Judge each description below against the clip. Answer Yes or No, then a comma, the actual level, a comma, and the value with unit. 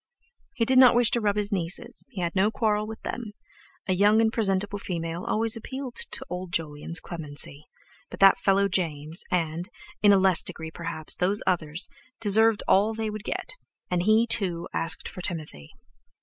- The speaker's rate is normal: Yes, average, 170 wpm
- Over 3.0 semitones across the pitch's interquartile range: Yes, average, 4.3 semitones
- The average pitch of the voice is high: Yes, high, 195 Hz